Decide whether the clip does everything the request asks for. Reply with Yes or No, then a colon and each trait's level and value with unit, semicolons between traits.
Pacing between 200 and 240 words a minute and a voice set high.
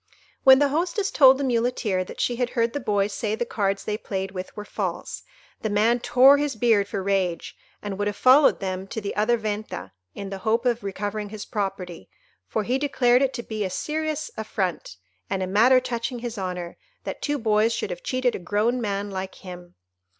Yes: fast, 205 wpm; high, 215 Hz